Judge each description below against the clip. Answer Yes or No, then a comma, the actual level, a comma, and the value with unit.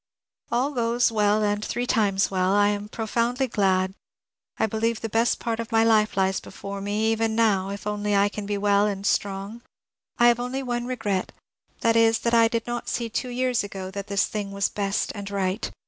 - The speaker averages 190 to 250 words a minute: Yes, fast, 205 wpm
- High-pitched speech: Yes, high, 215 Hz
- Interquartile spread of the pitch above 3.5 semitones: No, narrow, 2.6 semitones